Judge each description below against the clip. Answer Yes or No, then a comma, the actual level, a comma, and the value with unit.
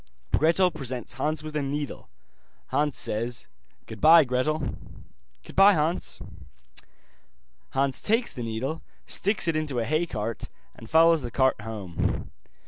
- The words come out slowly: Yes, slow, 130 wpm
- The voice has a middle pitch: Yes, medium, 145 Hz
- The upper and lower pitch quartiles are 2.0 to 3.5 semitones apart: No, average, 4.8 semitones